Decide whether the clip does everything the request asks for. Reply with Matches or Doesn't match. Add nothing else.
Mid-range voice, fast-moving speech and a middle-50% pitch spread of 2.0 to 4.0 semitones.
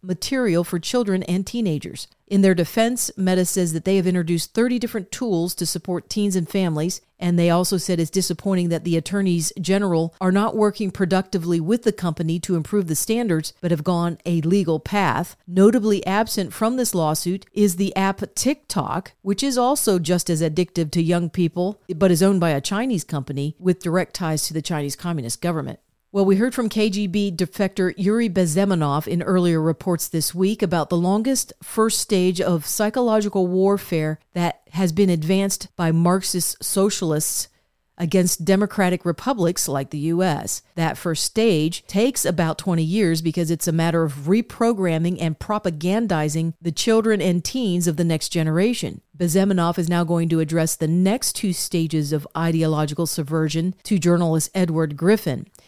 Doesn't match